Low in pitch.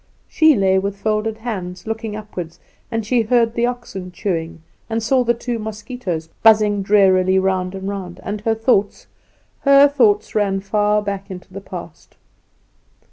No: high, 210 Hz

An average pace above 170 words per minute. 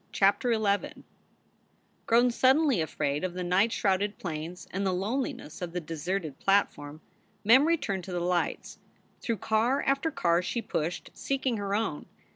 No: average, 150 wpm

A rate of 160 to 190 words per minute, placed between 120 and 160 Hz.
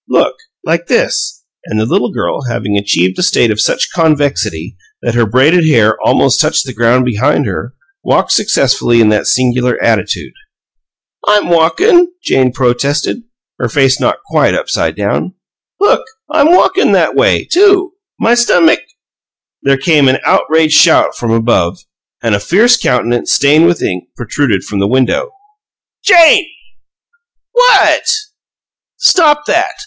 No: average, 145 wpm; medium, 140 Hz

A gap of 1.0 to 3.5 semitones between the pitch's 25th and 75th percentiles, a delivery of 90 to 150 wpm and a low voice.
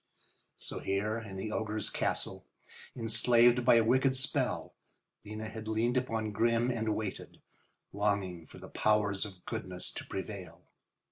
Yes: narrow, 2.4 semitones; average, 140 wpm; low, 110 Hz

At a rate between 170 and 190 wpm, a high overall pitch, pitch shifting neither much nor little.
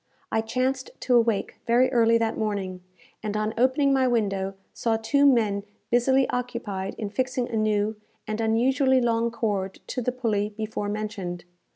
No: average, 160 wpm; high, 225 Hz; average, 3.1 semitones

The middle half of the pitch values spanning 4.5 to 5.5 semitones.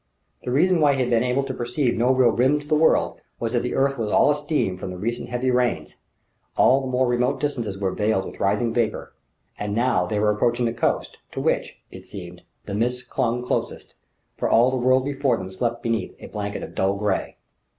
No: average, 3.6 semitones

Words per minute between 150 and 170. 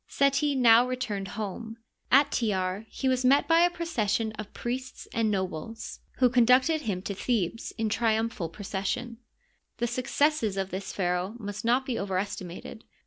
Yes: average, 160 wpm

